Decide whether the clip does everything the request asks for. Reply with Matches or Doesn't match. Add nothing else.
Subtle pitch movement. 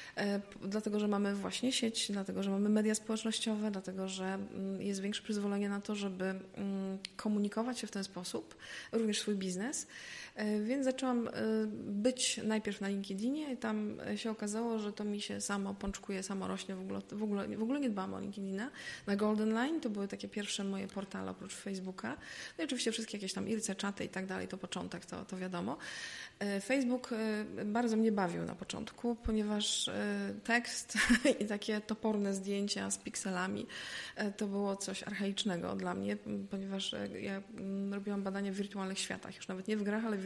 Matches